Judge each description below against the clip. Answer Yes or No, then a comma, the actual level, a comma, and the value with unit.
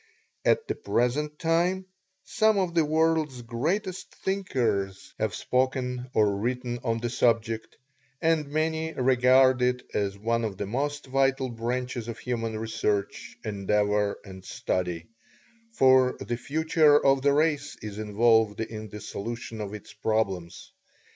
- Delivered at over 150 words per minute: No, slow, 135 wpm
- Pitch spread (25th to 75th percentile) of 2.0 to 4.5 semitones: No, average, 5.1 semitones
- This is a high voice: No, low, 125 Hz